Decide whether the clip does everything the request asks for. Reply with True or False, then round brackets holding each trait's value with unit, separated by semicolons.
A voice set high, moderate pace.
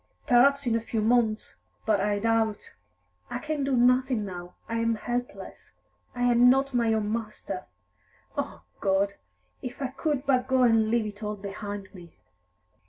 True (230 Hz; 165 wpm)